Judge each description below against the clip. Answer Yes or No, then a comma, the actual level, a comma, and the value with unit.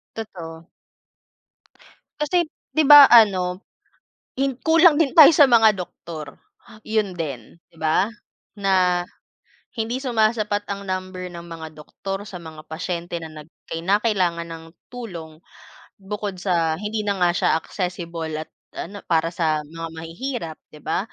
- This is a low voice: No, medium, 185 Hz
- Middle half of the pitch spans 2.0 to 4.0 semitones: No, average, 4.7 semitones